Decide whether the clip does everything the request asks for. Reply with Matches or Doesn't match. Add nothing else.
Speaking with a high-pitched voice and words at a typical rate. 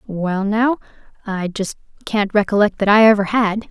Matches